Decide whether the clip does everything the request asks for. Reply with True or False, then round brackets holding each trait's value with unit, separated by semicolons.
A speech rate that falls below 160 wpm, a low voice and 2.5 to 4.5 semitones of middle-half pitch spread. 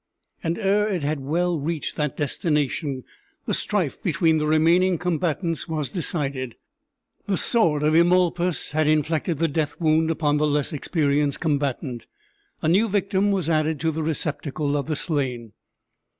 False (150 wpm; 155 Hz; 2.8 semitones)